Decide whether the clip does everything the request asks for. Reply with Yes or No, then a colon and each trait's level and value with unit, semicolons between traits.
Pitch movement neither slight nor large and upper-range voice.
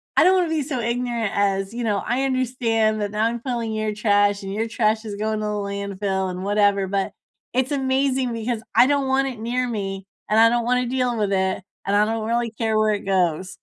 Yes: average, 3.3 semitones; high, 220 Hz